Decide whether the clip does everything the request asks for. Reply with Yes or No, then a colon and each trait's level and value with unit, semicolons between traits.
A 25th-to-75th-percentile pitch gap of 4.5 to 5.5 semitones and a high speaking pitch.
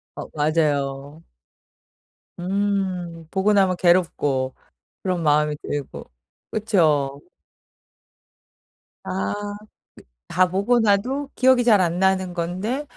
No: average, 5.1 semitones; medium, 180 Hz